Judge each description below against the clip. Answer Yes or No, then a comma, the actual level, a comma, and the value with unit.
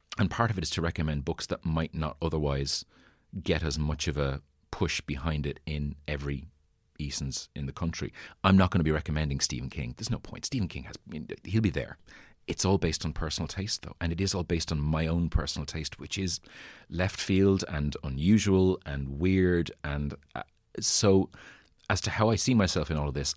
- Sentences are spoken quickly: Yes, fast, 215 wpm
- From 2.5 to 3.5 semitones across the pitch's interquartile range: No, average, 4.5 semitones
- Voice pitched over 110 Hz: No, very low, 80 Hz